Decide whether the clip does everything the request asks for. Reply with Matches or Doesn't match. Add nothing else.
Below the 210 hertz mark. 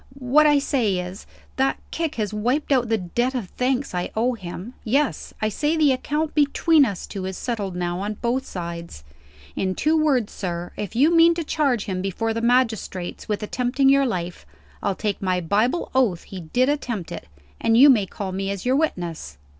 Doesn't match